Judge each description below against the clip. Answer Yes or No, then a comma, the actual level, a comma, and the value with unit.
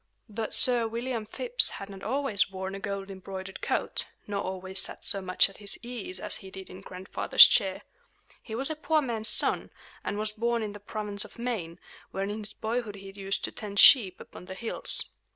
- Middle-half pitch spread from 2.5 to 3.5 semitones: Yes, average, 3.1 semitones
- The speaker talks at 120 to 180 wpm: No, fast, 205 wpm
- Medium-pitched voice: No, high, 205 Hz